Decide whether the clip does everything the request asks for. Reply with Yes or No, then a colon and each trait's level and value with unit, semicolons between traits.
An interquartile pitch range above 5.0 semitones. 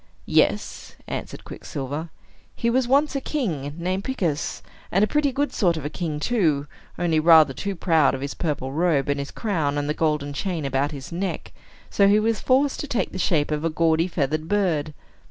Yes: wide, 5.6 semitones